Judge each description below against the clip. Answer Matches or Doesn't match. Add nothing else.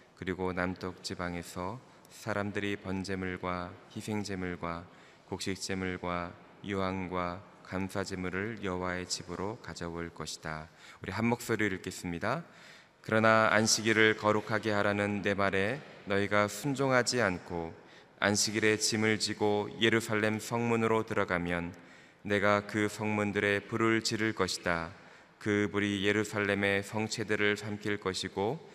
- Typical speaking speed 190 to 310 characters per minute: Matches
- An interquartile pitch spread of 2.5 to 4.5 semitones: Matches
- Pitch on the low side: Matches